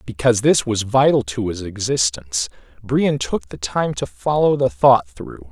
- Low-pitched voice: Yes, low, 110 Hz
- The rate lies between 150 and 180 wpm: Yes, average, 175 wpm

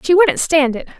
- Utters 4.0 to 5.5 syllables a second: Yes, 4.9 syllables/s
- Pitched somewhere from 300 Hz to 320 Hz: Yes, very high, 315 Hz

